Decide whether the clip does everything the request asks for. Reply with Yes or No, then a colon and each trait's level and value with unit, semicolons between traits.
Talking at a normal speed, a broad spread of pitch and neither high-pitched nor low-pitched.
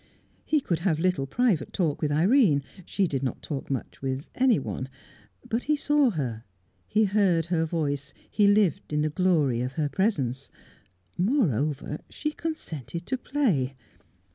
Yes: average, 150 wpm; wide, 7.1 semitones; medium, 165 Hz